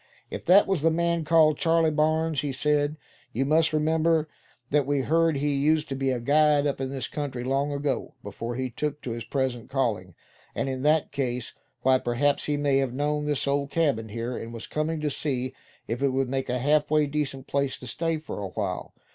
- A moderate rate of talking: No, fast, 215 wpm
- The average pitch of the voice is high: No, medium, 140 Hz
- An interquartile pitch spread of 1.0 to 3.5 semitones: Yes, average, 2.8 semitones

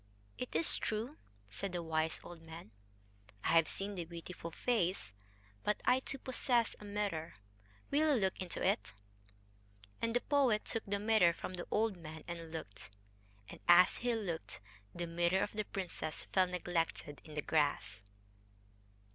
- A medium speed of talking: Yes, average, 160 wpm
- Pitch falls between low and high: Yes, medium, 180 Hz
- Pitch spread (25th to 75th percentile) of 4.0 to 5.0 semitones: Yes, average, 4.6 semitones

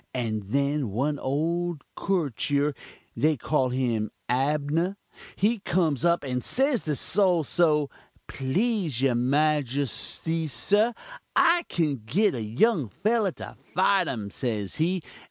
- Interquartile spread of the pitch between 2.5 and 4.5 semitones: No, wide, 5.6 semitones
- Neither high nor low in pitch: Yes, medium, 150 Hz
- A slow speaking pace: Yes, slow, 125 wpm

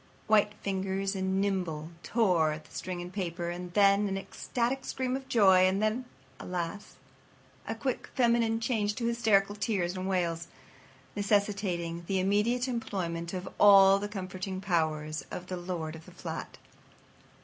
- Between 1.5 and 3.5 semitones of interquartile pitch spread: Yes, average, 3.1 semitones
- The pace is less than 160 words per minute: Yes, average, 150 wpm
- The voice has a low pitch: No, high, 195 Hz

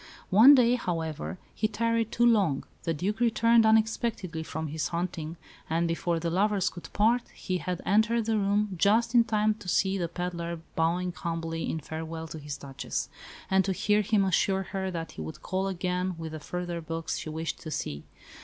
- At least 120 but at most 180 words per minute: No, average, 190 wpm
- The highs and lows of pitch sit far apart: No, average, 4.4 semitones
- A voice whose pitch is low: No, medium, 180 Hz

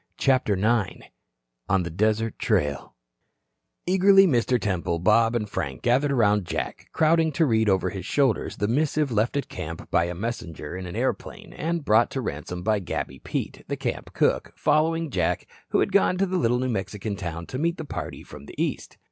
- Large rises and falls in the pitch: Yes, wide, 7.7 semitones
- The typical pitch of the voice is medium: No, low, 110 Hz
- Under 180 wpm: No, average, 190 wpm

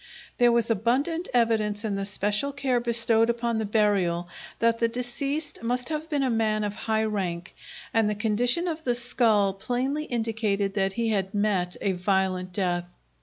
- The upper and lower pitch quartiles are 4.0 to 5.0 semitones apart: No, average, 3.3 semitones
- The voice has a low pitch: No, high, 225 Hz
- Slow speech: No, average, 170 wpm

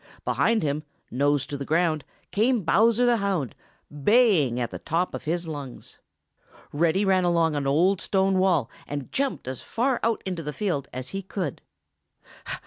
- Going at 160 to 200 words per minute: Yes, average, 165 wpm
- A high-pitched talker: No, medium, 170 Hz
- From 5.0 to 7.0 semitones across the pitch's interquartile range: Yes, wide, 5.5 semitones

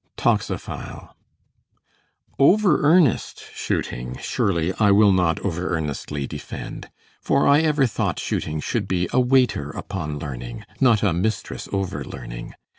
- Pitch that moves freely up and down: Yes, wide, 8.8 semitones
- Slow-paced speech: Yes, slow, 125 wpm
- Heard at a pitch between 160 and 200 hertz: No, very low, 95 Hz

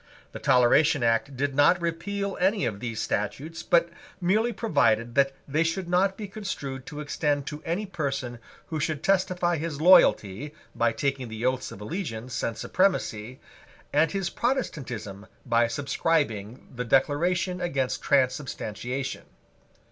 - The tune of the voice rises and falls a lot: Yes, wide, 6.1 semitones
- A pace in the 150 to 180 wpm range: No, average, 140 wpm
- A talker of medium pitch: Yes, medium, 145 Hz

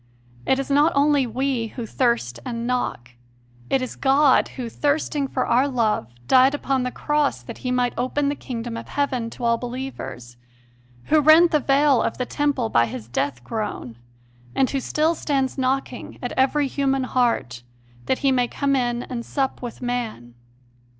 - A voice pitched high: Yes, very high, 255 Hz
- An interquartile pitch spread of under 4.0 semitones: Yes, average, 3.0 semitones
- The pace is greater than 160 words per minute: Yes, average, 175 wpm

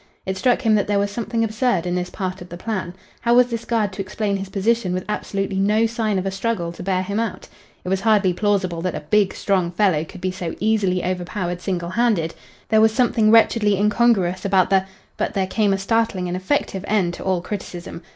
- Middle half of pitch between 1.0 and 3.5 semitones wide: Yes, average, 3.0 semitones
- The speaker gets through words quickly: Yes, fast, 220 wpm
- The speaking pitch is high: Yes, high, 195 Hz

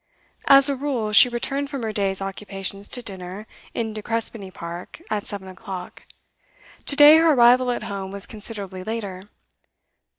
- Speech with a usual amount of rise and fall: Yes, average, 4.1 semitones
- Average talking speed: Yes, average, 160 wpm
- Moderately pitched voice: No, high, 210 Hz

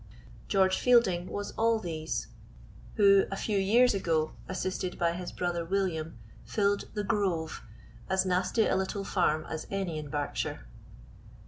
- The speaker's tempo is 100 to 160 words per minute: Yes, average, 140 wpm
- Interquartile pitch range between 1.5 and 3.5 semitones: Yes, average, 3.1 semitones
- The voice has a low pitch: No, high, 190 Hz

